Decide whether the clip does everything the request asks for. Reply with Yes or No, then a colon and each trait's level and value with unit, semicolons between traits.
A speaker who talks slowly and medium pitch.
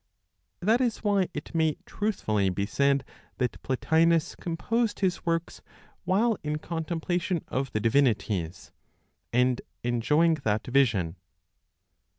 Yes: slow, 115 wpm; medium, 150 Hz